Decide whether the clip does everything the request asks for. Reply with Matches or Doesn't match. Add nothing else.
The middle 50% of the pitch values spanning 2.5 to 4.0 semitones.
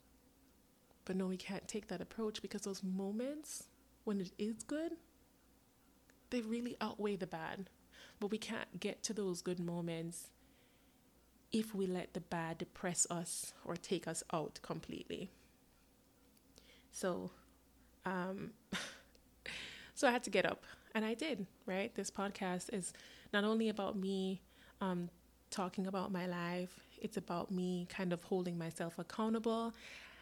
Matches